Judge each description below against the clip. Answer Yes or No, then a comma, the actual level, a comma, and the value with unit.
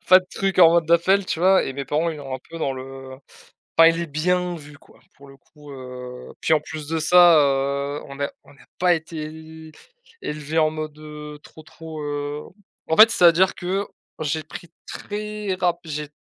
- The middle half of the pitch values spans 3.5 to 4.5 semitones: No, average, 3.0 semitones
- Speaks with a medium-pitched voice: Yes, medium, 155 Hz